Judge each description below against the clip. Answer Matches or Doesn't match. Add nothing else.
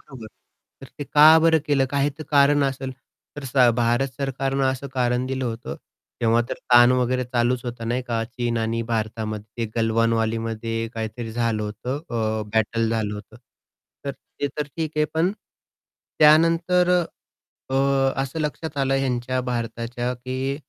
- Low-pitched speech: Matches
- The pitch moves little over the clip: Doesn't match